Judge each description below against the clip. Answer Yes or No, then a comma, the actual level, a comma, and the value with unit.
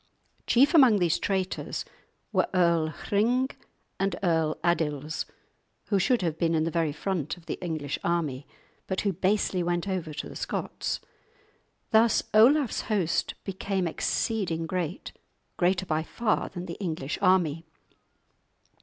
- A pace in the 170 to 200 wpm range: No, slow, 135 wpm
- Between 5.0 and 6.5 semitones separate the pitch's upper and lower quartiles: No, average, 3.5 semitones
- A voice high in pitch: No, medium, 175 Hz